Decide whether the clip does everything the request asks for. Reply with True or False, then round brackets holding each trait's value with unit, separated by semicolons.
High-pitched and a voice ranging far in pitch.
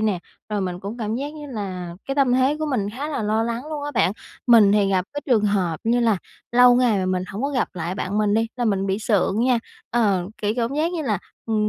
False (220 Hz; 4.2 semitones)